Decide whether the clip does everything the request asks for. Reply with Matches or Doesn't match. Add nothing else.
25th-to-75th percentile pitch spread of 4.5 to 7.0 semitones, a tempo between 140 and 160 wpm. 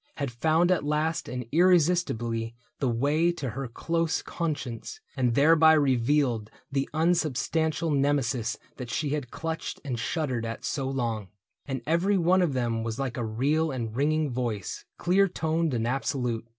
Matches